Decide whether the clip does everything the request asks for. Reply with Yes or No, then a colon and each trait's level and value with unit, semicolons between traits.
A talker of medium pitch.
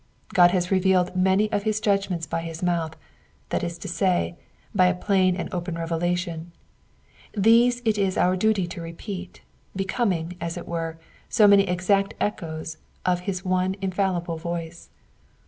Yes: medium, 180 Hz